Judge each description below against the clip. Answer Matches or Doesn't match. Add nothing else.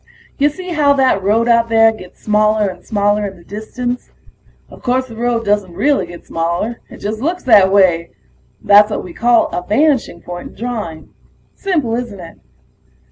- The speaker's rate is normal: Matches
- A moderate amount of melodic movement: Matches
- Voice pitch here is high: Matches